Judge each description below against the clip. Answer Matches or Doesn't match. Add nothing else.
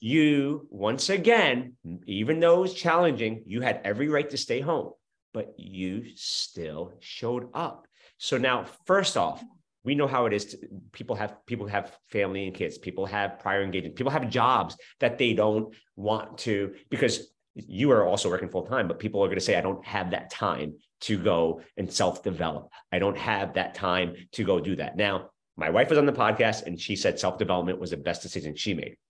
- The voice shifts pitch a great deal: Matches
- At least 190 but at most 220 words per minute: Matches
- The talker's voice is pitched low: Matches